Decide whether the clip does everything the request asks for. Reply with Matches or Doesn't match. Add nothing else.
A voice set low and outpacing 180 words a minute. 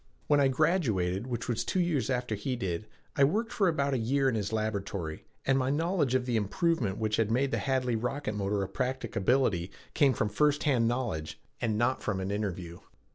Matches